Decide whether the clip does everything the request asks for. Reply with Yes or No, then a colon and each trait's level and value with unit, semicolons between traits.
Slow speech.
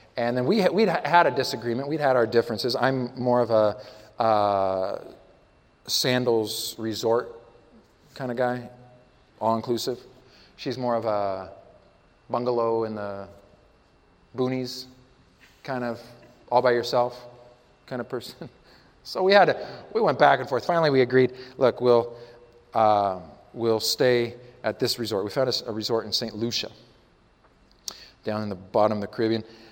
No: average, 150 wpm